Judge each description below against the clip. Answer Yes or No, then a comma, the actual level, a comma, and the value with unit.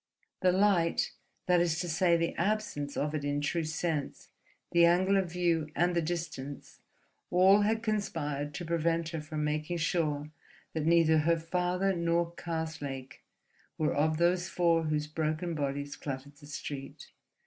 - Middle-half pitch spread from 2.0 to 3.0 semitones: Yes, average, 2.7 semitones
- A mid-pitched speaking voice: Yes, medium, 165 Hz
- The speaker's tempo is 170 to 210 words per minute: No, average, 155 wpm